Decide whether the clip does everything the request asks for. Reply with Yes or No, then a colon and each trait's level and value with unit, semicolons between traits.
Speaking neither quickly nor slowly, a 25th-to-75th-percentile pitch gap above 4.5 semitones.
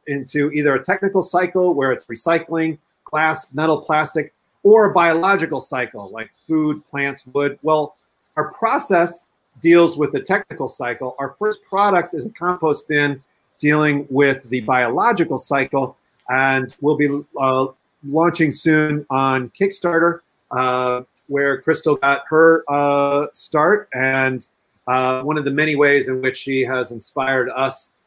No: average, 145 wpm; average, 3.5 semitones